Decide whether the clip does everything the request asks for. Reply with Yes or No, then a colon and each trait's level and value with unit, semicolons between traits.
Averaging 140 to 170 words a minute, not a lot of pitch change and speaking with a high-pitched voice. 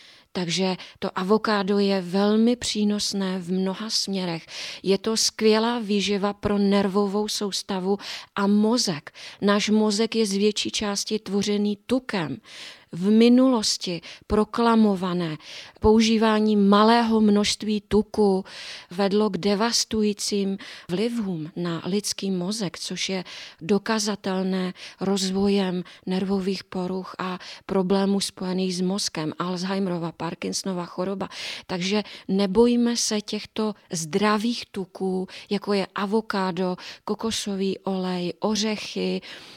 No: slow, 100 wpm; narrow, 2.2 semitones; high, 200 Hz